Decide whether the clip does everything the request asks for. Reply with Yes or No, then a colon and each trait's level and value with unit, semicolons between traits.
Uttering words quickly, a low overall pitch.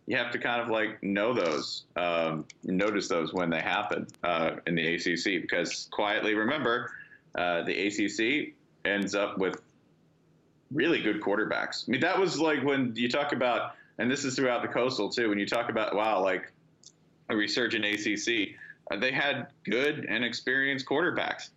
No: average, 170 wpm; low, 120 Hz